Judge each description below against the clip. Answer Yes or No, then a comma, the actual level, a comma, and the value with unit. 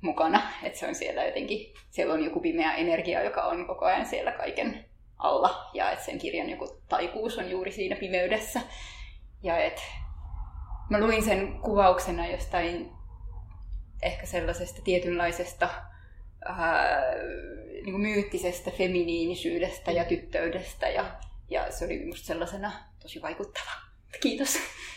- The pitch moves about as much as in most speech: No, wide, 7.6 semitones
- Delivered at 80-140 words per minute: Yes, average, 130 wpm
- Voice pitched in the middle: Yes, medium, 180 Hz